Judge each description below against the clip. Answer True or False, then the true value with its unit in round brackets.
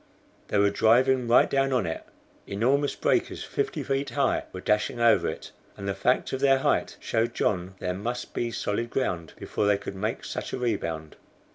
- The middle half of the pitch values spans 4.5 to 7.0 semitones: True (4.9 semitones)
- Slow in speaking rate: False (185 wpm)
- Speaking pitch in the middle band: False (115 Hz)